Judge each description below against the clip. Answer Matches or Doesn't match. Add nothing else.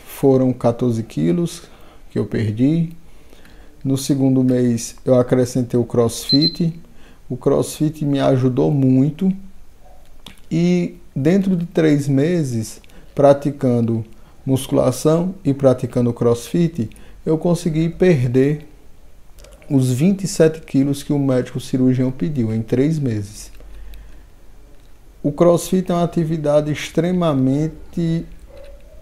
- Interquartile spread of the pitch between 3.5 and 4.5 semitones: Doesn't match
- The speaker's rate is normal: Doesn't match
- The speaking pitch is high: Doesn't match